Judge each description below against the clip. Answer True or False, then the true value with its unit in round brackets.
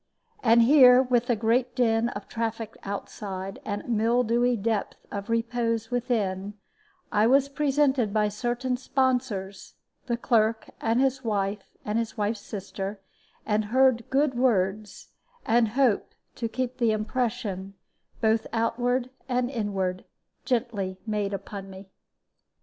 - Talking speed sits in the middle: False (130 wpm)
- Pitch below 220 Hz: False (230 Hz)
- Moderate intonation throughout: True (3.1 semitones)